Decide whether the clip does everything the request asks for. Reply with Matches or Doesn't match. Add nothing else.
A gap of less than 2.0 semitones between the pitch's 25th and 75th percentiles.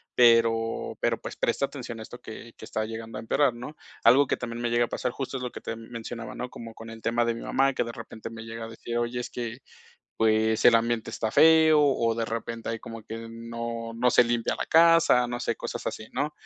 Matches